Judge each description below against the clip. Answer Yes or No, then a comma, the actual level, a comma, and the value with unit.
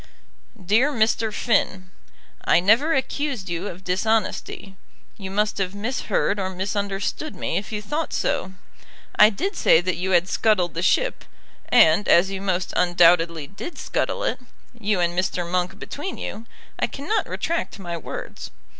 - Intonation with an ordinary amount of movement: Yes, average, 3.7 semitones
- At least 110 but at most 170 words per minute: Yes, average, 155 wpm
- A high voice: Yes, high, 195 Hz